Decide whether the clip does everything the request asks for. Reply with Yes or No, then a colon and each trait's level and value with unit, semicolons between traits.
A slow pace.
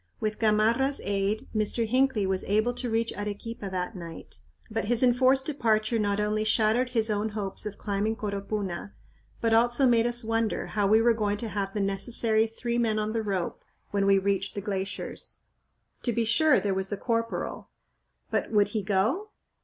No: average, 180 wpm